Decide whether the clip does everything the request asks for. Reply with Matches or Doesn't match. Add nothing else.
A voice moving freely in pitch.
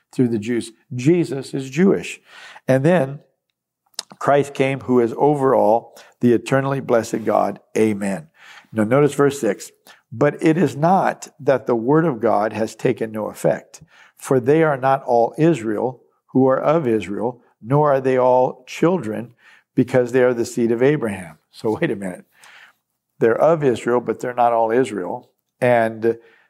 Doesn't match